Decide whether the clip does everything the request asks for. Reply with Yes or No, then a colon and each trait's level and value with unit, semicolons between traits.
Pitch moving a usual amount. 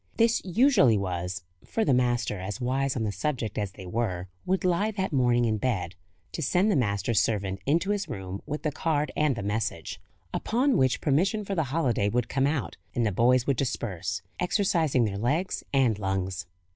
No: wide, 8.0 semitones